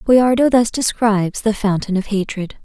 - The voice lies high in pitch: Yes, high, 215 Hz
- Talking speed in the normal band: Yes, average, 160 wpm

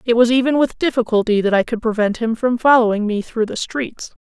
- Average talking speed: No, fast, 225 wpm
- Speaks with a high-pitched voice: Yes, high, 235 Hz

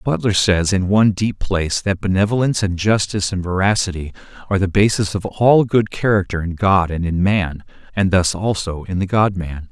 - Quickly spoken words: No, average, 190 wpm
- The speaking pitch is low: Yes, very low, 95 Hz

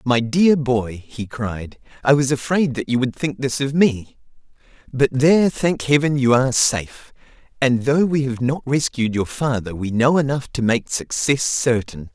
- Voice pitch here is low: Yes, low, 130 Hz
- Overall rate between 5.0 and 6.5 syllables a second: No, 4.5 syllables/s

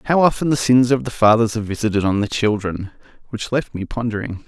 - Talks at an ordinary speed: No, fast, 215 wpm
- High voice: No, low, 115 Hz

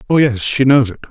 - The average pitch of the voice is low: Yes, low, 125 Hz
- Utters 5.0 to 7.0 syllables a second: Yes, 6.0 syllables/s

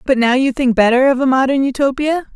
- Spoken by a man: No, female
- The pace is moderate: No, fast, 230 wpm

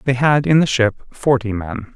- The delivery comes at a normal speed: No, fast, 215 wpm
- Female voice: No, male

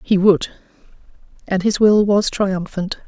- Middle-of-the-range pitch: No, high, 195 Hz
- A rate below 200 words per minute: Yes, slow, 135 wpm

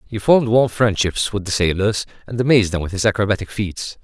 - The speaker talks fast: Yes, fast, 210 wpm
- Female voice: No, male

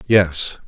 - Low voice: Yes, very low, 90 Hz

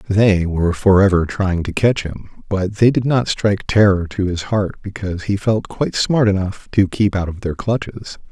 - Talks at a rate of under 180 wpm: No, average, 200 wpm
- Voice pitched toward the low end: Yes, low, 100 Hz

